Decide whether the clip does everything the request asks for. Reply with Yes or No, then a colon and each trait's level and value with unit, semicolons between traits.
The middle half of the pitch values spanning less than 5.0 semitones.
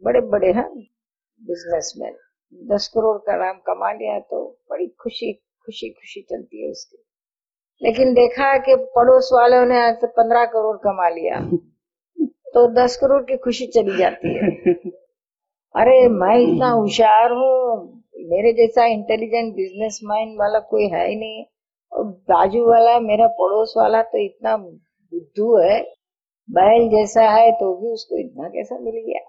Yes: average, 3.7 semitones